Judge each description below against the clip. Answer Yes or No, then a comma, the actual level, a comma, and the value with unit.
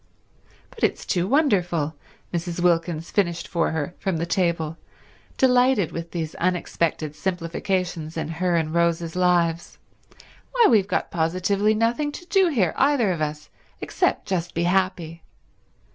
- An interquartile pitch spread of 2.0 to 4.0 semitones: Yes, average, 3.0 semitones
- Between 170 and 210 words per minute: No, average, 140 wpm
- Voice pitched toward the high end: No, medium, 175 Hz